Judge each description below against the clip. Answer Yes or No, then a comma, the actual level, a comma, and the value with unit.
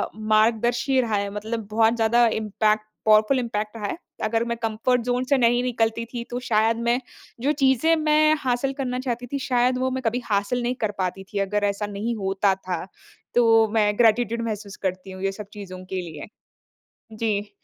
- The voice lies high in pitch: Yes, high, 225 Hz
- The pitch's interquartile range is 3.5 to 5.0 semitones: No, average, 2.8 semitones